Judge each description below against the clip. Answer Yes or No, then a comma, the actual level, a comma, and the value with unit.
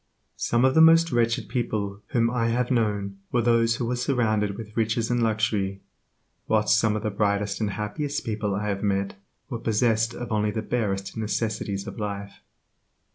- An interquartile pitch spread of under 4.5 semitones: Yes, narrow, 2.4 semitones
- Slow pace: No, average, 180 wpm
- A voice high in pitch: No, low, 110 Hz